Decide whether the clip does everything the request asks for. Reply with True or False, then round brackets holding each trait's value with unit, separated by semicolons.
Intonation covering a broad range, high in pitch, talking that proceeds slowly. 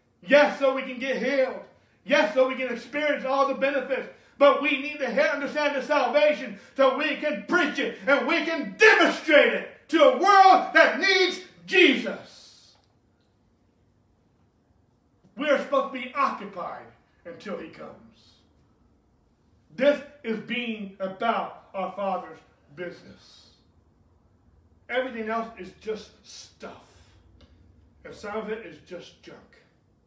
True (7.9 semitones; 260 Hz; 130 wpm)